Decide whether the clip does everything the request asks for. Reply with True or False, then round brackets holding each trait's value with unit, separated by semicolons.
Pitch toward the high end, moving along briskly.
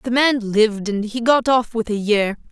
True (225 Hz; 240 wpm)